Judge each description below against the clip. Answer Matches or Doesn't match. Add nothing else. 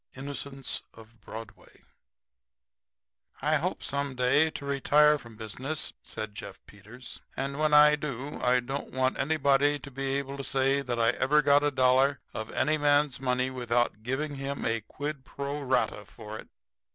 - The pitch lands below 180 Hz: Matches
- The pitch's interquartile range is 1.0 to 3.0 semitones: Matches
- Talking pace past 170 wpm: Doesn't match